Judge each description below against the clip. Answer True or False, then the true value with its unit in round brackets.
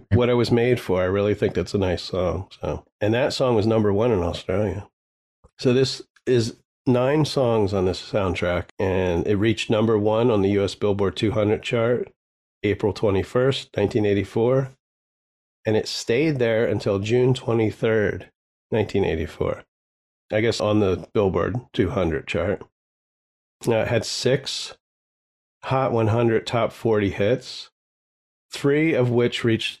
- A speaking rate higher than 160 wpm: False (145 wpm)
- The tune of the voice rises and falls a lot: False (3.8 semitones)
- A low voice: True (110 Hz)